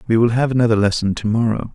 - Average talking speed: No, fast, 240 wpm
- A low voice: Yes, low, 115 Hz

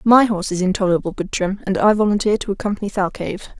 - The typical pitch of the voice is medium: No, high, 200 Hz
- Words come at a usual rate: No, fast, 215 wpm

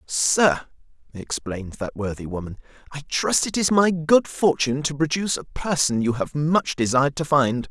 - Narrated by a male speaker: Yes, male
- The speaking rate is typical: Yes, average, 170 wpm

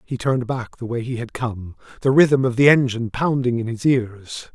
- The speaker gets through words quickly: Yes, fast, 225 wpm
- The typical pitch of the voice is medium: No, low, 125 Hz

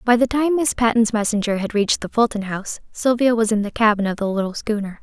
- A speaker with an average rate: No, fast, 240 wpm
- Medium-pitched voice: No, high, 220 Hz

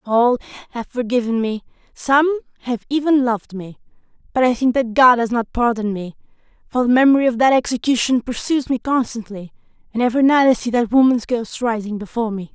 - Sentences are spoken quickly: No, average, 180 wpm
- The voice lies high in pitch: Yes, high, 240 Hz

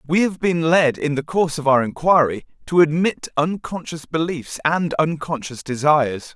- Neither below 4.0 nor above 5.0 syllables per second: Yes, 4.8 syllables/s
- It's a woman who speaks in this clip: No, male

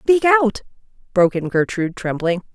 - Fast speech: No, average, 140 wpm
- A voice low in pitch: No, high, 215 Hz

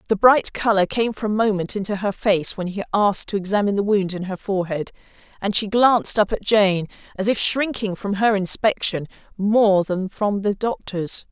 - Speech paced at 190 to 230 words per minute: Yes, average, 195 wpm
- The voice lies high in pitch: Yes, high, 200 Hz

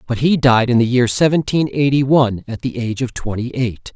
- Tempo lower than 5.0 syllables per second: No, 5.6 syllables/s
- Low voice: Yes, low, 125 Hz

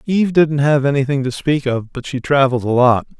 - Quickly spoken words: Yes, fast, 225 wpm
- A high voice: No, low, 135 Hz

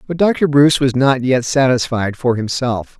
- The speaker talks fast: No, average, 180 wpm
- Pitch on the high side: No, low, 130 Hz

